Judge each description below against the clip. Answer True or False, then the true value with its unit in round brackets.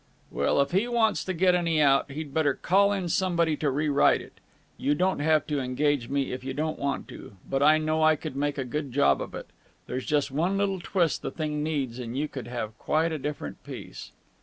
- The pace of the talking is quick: True (225 wpm)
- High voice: False (150 Hz)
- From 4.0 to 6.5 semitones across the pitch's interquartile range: False (3.2 semitones)